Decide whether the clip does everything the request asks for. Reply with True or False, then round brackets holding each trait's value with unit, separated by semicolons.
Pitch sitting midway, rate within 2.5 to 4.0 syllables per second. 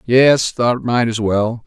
False (120 Hz; 3.2 syllables/s)